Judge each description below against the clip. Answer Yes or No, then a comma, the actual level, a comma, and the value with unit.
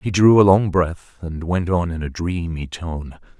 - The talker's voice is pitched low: Yes, very low, 85 Hz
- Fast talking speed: Yes, fast, 210 wpm